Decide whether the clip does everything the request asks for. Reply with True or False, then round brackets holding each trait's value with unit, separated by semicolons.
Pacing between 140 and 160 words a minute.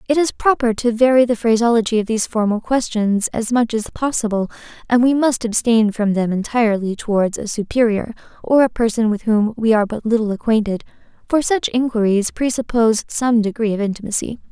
False (180 wpm)